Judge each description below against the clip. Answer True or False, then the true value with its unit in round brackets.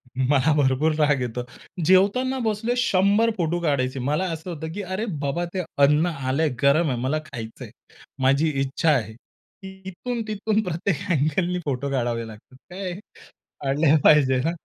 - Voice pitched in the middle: True (155 Hz)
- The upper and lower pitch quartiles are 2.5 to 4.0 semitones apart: False (5.5 semitones)